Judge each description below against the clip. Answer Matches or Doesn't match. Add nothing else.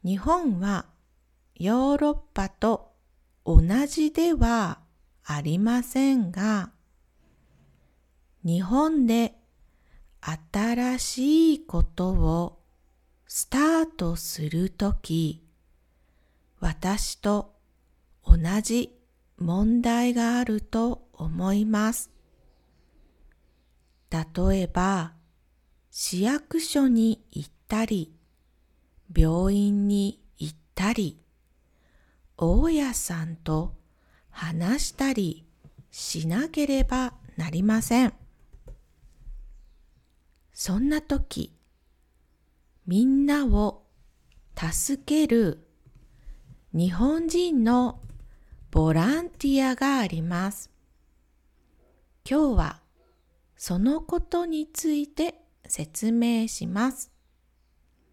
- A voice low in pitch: Doesn't match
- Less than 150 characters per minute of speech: Matches